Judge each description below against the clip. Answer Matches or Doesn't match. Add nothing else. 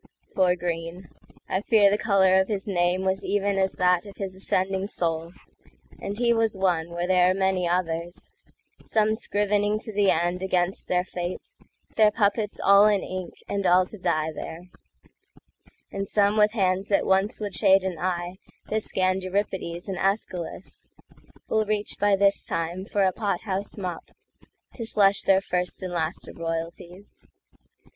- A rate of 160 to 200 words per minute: Doesn't match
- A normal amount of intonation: Doesn't match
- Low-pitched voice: Doesn't match